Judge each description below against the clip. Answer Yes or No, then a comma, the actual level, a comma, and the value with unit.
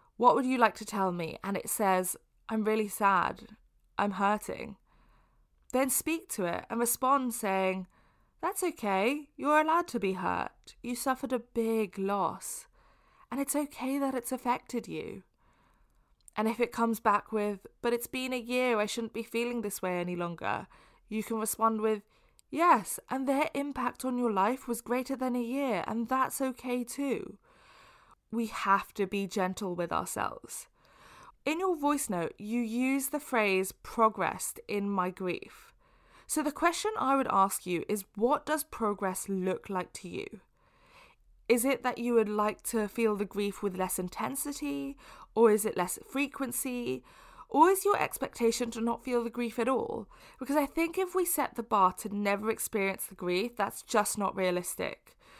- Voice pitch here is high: Yes, high, 230 Hz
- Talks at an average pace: Yes, average, 175 wpm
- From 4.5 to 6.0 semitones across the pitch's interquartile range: Yes, average, 5.0 semitones